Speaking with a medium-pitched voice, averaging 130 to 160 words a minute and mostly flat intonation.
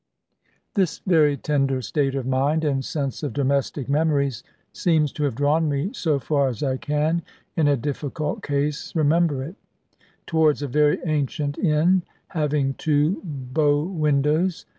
Yes: medium, 150 Hz; average, 145 wpm; narrow, 2.1 semitones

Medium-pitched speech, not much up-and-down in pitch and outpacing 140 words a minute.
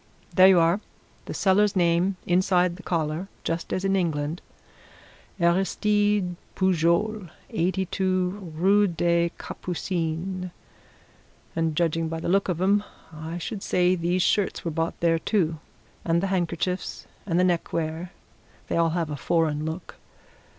No: medium, 175 Hz; narrow, 2.3 semitones; slow, 135 wpm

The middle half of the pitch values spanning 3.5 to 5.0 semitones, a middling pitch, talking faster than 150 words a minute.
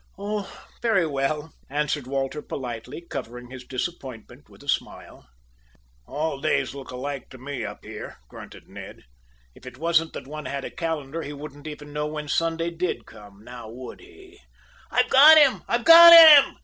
Yes: average, 4.6 semitones; medium, 150 Hz; average, 175 wpm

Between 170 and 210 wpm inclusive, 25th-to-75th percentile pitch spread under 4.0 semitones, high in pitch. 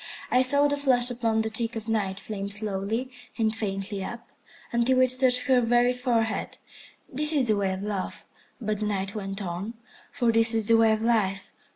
Yes: average, 195 wpm; average, 3.3 semitones; high, 225 Hz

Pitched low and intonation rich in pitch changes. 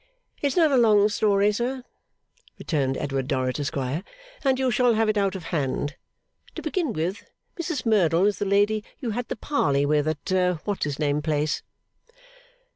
No: high, 195 Hz; wide, 7.2 semitones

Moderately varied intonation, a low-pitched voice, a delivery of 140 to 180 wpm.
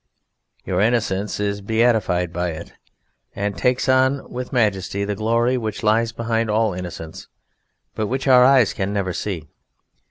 Yes: average, 3.7 semitones; low, 110 Hz; average, 150 wpm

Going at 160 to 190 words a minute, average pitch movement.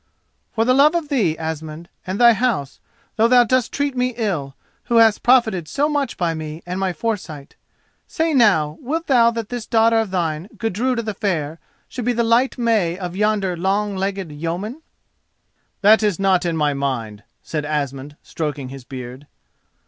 No: average, 170 wpm; wide, 6.8 semitones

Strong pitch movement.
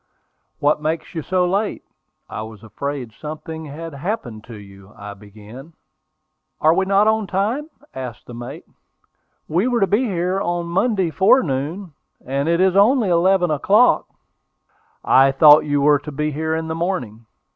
Yes: wide, 6.0 semitones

